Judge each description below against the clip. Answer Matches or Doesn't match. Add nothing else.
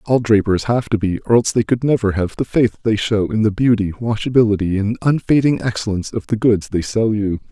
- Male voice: Matches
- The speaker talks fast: Matches